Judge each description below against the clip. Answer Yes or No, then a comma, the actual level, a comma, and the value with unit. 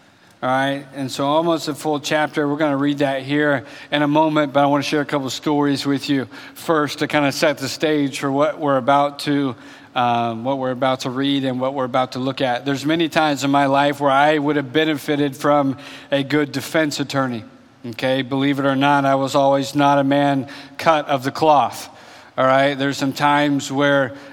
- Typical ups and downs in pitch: No, narrow, 1.4 semitones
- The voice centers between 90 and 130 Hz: No, medium, 140 Hz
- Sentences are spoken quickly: Yes, fast, 220 wpm